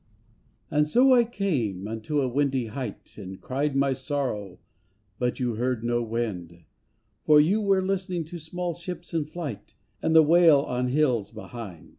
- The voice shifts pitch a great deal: Yes, wide, 6.1 semitones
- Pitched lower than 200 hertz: Yes, low, 135 Hz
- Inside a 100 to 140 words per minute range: No, average, 160 wpm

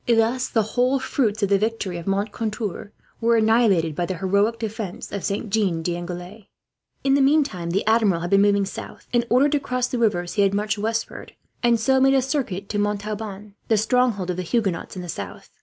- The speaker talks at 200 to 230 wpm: Yes, fast, 205 wpm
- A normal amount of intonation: Yes, average, 3.5 semitones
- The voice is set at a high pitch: Yes, high, 210 Hz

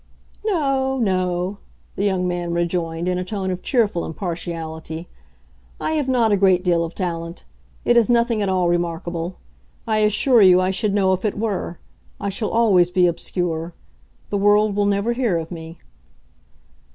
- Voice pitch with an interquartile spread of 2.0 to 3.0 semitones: No, average, 3.6 semitones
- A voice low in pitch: No, medium, 185 Hz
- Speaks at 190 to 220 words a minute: No, average, 165 wpm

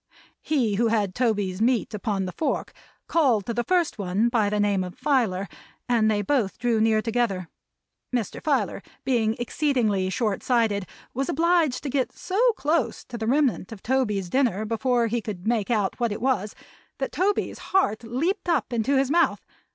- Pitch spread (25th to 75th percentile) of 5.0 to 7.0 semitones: No, average, 4.3 semitones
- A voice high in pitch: Yes, high, 235 Hz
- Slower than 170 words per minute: No, average, 175 wpm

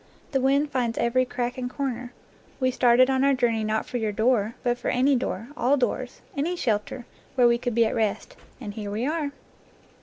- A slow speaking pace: No, fast, 205 wpm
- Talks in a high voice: Yes, high, 245 Hz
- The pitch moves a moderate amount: No, narrow, 2.3 semitones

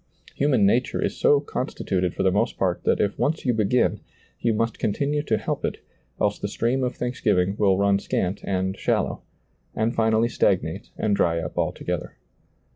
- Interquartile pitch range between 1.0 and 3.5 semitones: No, average, 4.0 semitones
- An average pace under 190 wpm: Yes, average, 180 wpm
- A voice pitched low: Yes, low, 110 Hz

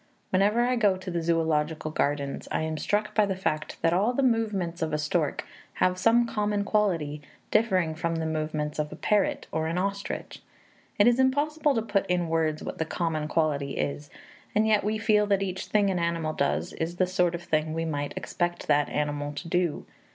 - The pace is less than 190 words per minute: No, fast, 205 wpm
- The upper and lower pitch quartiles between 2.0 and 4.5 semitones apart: No, average, 4.9 semitones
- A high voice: No, medium, 175 Hz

